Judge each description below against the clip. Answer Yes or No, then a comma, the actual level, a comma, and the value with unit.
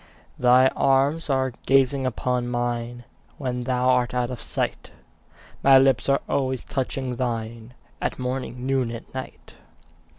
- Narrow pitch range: Yes, narrow, 1.5 semitones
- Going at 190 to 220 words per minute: No, slow, 135 wpm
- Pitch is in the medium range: No, low, 125 Hz